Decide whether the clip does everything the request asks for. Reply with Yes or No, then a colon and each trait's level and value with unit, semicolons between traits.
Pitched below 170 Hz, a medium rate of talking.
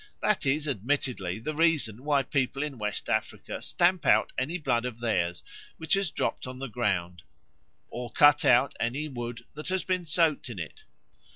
Yes: low, 135 Hz; average, 175 wpm